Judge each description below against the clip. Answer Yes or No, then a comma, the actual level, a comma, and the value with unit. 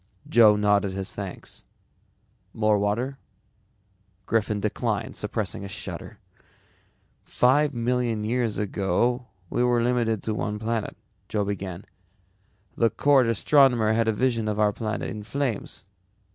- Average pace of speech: No, slow, 125 wpm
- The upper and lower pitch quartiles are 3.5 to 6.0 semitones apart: No, average, 2.8 semitones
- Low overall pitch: Yes, low, 110 Hz